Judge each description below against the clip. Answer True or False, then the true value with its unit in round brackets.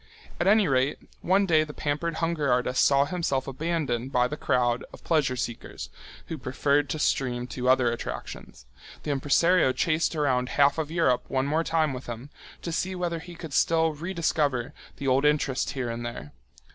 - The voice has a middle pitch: True (145 Hz)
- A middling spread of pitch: True (4.2 semitones)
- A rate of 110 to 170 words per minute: False (185 wpm)